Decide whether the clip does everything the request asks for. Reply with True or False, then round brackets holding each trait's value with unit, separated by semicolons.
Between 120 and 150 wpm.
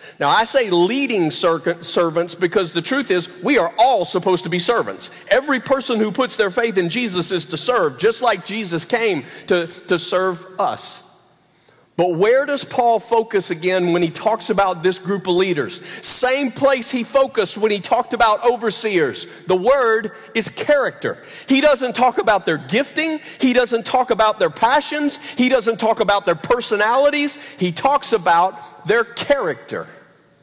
False (170 wpm)